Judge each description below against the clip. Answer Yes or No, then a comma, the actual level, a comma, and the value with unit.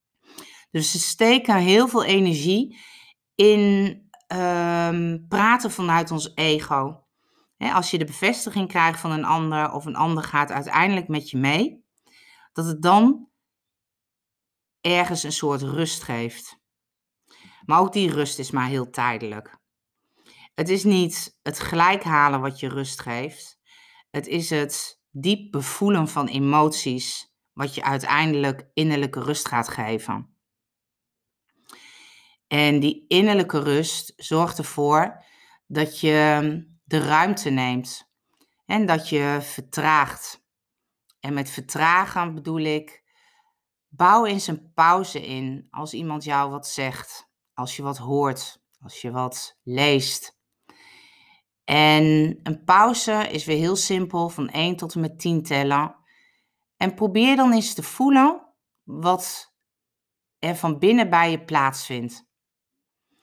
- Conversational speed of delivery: No, slow, 125 wpm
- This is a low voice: No, medium, 155 Hz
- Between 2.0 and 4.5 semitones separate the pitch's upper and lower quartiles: No, average, 4.9 semitones